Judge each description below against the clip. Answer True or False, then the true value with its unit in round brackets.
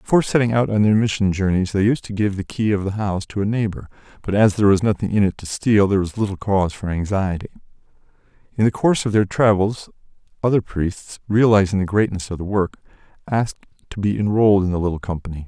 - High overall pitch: False (100 Hz)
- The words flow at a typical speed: False (215 wpm)